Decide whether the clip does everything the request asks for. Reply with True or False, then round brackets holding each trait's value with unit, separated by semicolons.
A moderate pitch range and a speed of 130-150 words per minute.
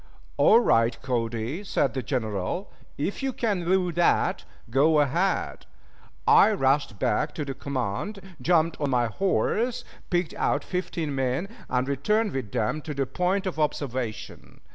False (6.2 semitones; 145 wpm)